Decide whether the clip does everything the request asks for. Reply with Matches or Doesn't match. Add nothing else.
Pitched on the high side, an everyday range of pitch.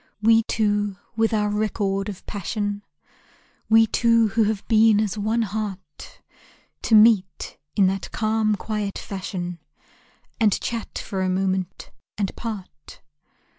Doesn't match